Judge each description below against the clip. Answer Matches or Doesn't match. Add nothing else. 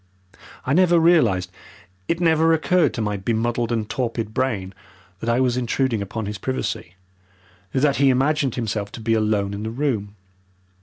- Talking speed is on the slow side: Doesn't match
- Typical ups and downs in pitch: Matches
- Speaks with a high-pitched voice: Doesn't match